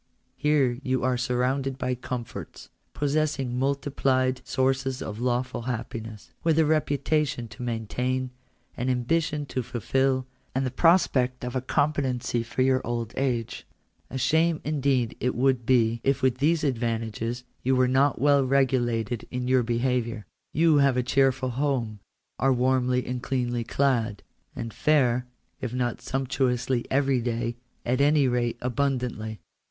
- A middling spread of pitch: No, narrow, 2.1 semitones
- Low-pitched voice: Yes, low, 130 Hz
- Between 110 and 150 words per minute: Yes, average, 145 wpm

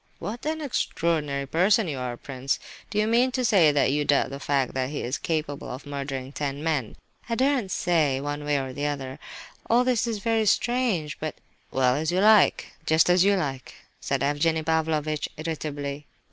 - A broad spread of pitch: Yes, wide, 6.0 semitones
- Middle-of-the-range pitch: Yes, medium, 155 Hz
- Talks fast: No, average, 185 wpm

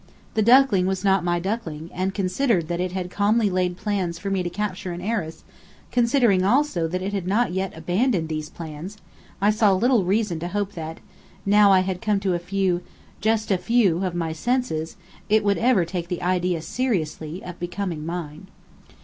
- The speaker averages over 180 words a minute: Yes, average, 190 wpm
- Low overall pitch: No, medium, 185 Hz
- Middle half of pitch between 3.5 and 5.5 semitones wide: No, average, 3.1 semitones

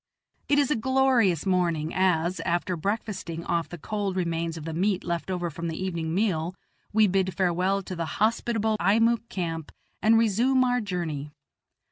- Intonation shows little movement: No, average, 4.4 semitones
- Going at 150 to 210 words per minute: Yes, average, 165 wpm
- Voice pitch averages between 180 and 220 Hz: Yes, medium, 185 Hz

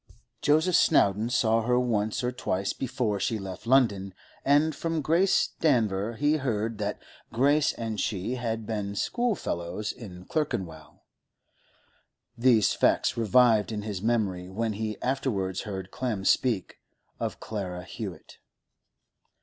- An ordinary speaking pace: No, slow, 125 wpm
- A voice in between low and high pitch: No, low, 110 Hz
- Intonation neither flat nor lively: Yes, average, 4.3 semitones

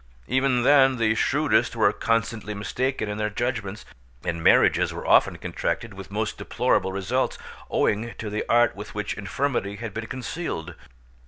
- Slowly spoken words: No, average, 155 wpm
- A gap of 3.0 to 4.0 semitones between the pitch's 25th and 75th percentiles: Yes, average, 3.3 semitones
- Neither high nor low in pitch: No, low, 110 Hz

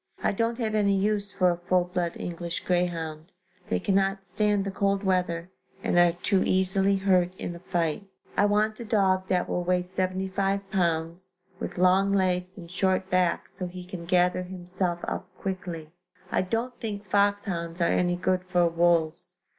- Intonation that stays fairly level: Yes, narrow, 1.9 semitones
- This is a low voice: No, medium, 185 Hz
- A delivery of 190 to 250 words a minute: No, average, 170 wpm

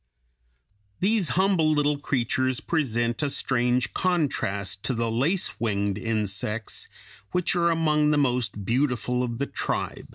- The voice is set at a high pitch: No, low, 130 Hz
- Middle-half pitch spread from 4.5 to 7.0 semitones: Yes, average, 5.1 semitones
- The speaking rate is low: Yes, slow, 130 wpm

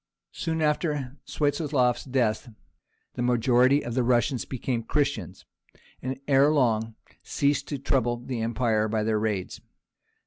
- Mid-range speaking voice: No, low, 125 Hz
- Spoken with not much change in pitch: No, average, 3.6 semitones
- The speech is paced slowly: Yes, slow, 130 wpm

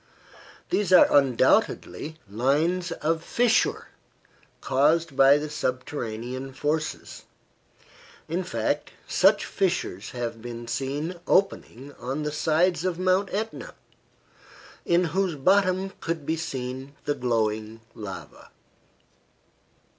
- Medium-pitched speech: Yes, medium, 150 Hz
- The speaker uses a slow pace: Yes, slow, 100 wpm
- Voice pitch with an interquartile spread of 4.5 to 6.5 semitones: Yes, wide, 5.6 semitones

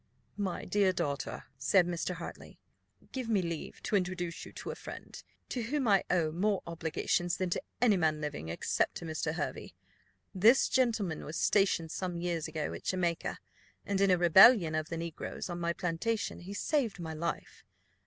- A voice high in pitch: No, medium, 175 Hz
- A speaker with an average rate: Yes, average, 175 wpm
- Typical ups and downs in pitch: Yes, average, 3.3 semitones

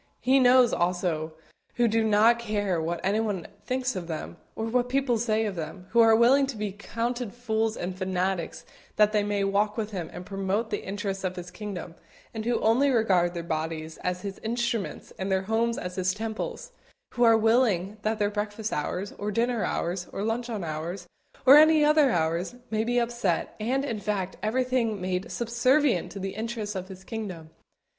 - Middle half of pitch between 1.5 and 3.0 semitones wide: No, average, 4.0 semitones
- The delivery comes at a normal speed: Yes, average, 185 wpm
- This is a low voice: No, high, 210 Hz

